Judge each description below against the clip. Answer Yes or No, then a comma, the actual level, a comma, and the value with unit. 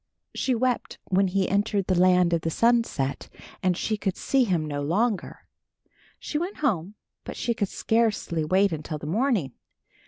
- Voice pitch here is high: Yes, high, 195 Hz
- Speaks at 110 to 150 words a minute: No, average, 165 wpm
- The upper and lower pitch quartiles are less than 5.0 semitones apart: No, wide, 5.4 semitones